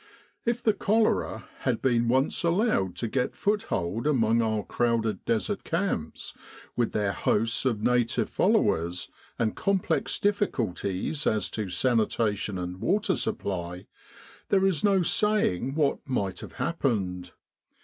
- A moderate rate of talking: No, slow, 130 wpm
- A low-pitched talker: Yes, low, 115 Hz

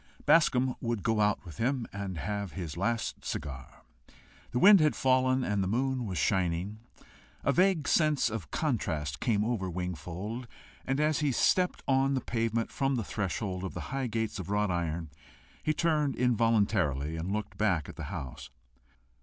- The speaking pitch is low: Yes, low, 110 Hz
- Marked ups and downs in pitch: Yes, wide, 6.1 semitones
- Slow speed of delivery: No, average, 170 wpm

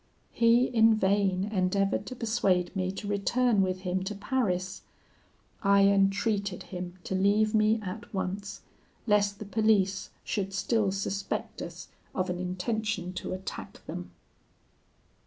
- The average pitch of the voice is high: Yes, high, 200 Hz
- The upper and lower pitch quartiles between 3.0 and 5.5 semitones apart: No, narrow, 2.4 semitones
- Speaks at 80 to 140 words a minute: Yes, slow, 135 wpm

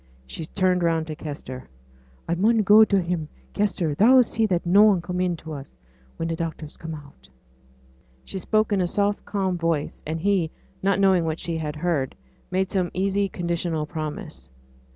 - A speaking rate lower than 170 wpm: No, average, 175 wpm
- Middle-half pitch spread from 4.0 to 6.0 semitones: No, average, 3.6 semitones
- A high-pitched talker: No, medium, 175 Hz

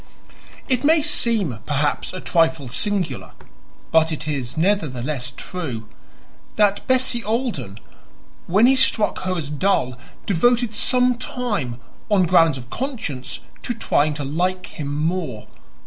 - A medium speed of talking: No, slow, 130 wpm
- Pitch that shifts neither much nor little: No, wide, 7.6 semitones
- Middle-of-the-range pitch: Yes, medium, 175 Hz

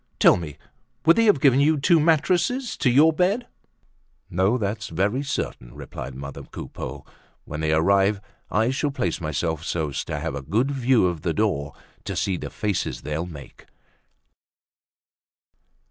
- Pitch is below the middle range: Yes, low, 100 Hz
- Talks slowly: No, average, 160 wpm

